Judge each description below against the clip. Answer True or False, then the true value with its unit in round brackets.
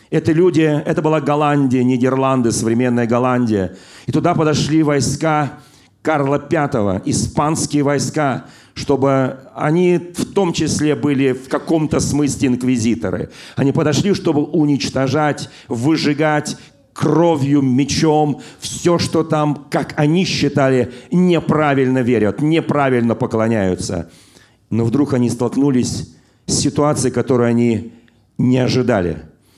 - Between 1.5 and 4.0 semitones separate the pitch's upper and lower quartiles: True (3.7 semitones)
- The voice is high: False (140 Hz)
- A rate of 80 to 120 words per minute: True (110 wpm)